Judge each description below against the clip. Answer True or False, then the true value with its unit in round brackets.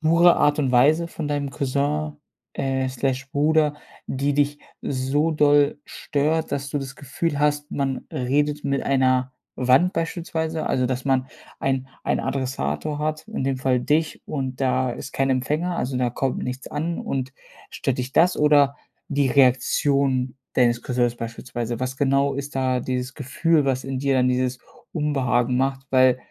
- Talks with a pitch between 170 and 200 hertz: False (135 Hz)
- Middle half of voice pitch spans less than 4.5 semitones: True (2.4 semitones)